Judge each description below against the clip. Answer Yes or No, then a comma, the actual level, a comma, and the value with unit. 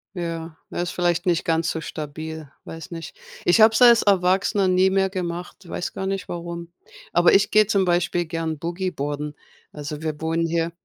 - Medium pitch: Yes, medium, 170 Hz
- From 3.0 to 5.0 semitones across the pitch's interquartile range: No, narrow, 2.4 semitones